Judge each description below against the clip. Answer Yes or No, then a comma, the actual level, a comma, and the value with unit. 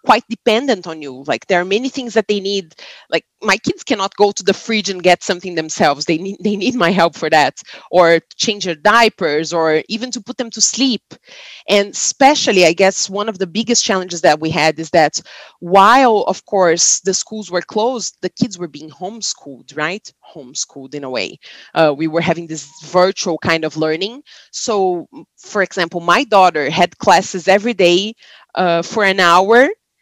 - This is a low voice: No, high, 190 Hz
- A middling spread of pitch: Yes, average, 4.6 semitones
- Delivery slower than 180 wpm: No, average, 190 wpm